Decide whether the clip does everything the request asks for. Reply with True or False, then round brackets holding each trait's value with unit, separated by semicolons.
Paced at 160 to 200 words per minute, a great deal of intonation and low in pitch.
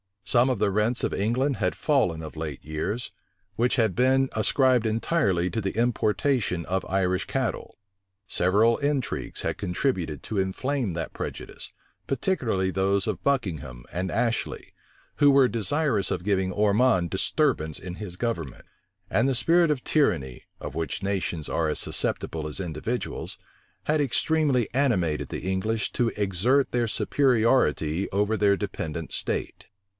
False (145 wpm; 5.9 semitones; 105 Hz)